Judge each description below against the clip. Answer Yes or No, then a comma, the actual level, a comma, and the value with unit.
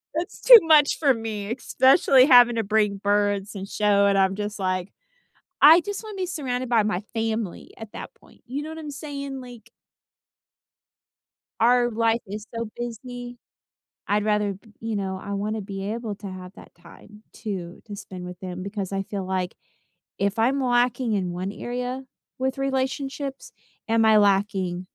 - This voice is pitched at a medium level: No, high, 220 Hz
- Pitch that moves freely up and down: No, average, 4.2 semitones